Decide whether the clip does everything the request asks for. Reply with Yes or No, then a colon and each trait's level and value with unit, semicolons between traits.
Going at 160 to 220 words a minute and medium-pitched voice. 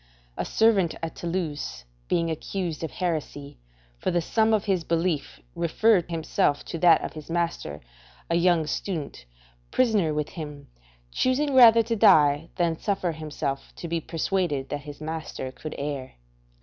No: average, 150 wpm; medium, 165 Hz